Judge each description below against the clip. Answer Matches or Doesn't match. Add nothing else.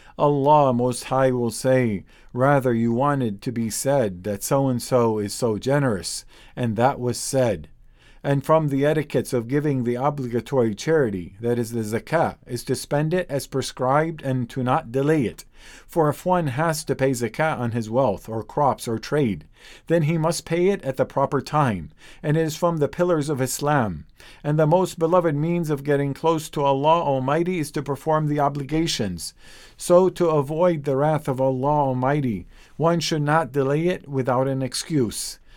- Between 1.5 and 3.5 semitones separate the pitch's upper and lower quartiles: Doesn't match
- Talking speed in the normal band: Matches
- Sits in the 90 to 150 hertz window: Matches